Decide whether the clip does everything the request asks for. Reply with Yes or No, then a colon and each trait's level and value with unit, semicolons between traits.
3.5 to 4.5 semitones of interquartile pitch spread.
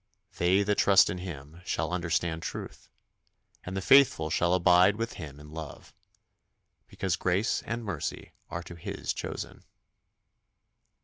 No: average, 2.9 semitones